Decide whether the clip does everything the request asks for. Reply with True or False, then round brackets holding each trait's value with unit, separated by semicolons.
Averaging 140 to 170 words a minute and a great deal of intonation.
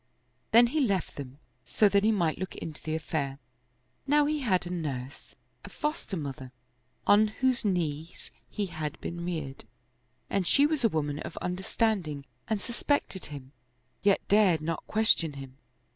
True (155 wpm; 6.3 semitones)